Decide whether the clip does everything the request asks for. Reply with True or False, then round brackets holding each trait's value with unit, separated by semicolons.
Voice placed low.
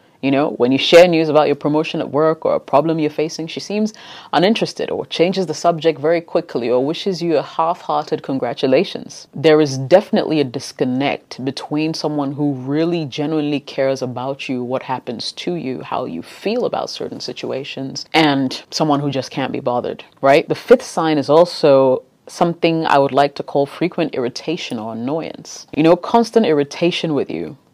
False (155 Hz)